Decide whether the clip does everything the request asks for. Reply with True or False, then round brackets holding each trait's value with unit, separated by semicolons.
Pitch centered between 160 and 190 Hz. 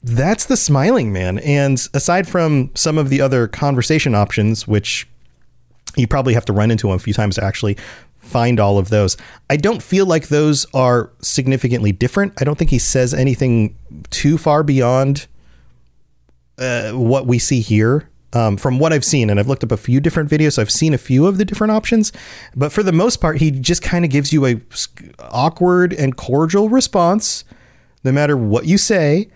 False (135 Hz)